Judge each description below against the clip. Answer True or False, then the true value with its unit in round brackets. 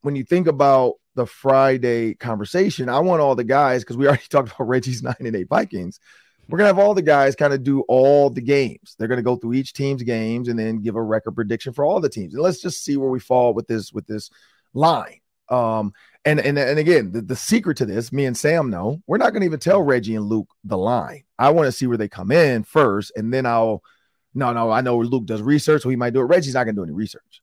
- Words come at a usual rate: False (255 wpm)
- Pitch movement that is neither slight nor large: True (3.7 semitones)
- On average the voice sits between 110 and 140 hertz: True (130 Hz)